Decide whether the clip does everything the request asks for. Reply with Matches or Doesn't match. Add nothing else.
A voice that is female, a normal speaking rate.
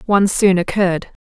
Matches